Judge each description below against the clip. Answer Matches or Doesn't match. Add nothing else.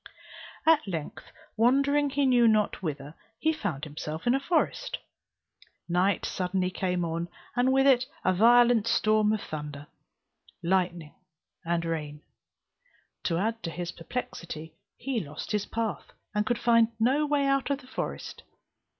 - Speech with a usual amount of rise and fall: Doesn't match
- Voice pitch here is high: Matches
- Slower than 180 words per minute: Matches